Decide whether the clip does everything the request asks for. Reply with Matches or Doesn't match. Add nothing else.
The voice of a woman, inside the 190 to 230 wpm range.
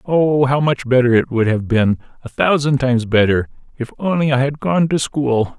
Doesn't match